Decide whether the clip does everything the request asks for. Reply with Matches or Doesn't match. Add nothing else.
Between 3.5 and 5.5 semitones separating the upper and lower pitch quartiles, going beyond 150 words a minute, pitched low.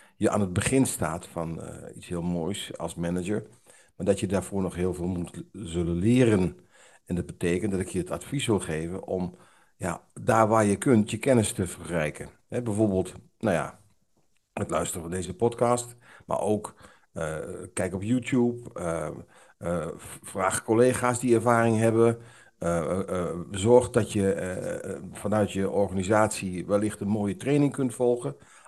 Matches